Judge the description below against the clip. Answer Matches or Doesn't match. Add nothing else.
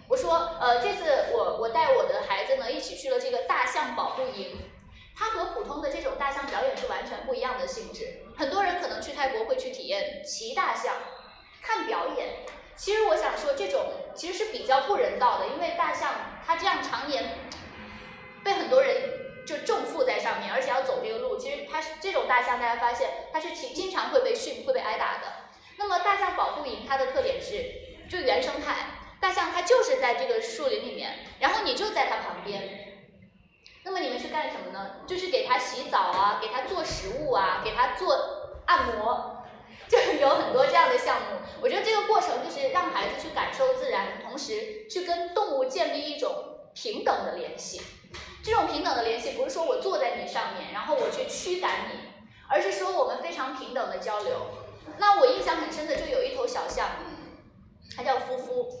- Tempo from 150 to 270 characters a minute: Doesn't match